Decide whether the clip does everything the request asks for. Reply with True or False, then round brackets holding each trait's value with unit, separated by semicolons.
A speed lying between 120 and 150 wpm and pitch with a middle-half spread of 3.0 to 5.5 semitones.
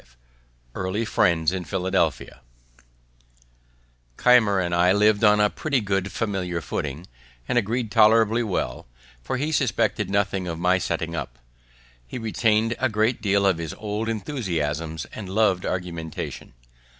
True (140 wpm; 4.2 semitones)